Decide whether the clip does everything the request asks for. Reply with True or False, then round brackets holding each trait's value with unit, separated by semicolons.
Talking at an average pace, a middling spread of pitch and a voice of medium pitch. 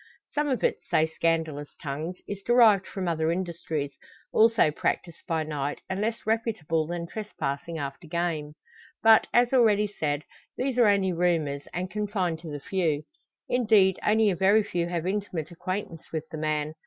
True (165 wpm; 4.8 semitones; 175 Hz)